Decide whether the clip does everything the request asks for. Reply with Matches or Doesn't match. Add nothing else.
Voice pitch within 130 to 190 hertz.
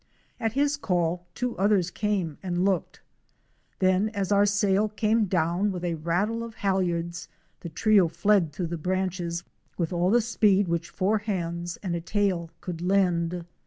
Matches